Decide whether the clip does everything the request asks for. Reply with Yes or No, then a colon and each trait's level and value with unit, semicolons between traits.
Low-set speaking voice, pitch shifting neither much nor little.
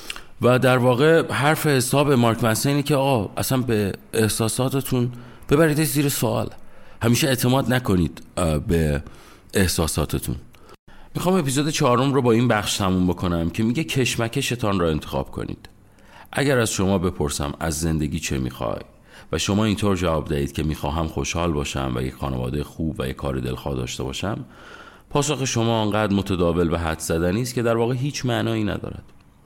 No: low, 105 Hz; wide, 7.8 semitones